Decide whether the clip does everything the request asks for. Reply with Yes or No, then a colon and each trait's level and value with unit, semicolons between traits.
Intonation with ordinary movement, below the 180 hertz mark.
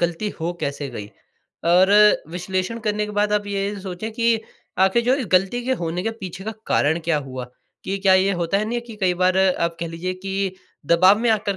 No: average, 3.4 semitones; high, 190 Hz